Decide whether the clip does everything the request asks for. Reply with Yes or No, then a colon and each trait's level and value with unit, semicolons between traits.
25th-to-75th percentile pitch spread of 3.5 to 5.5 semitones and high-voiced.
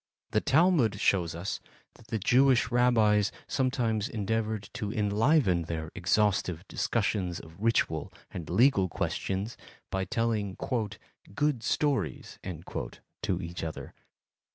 No: average, 4.2 semitones; low, 105 Hz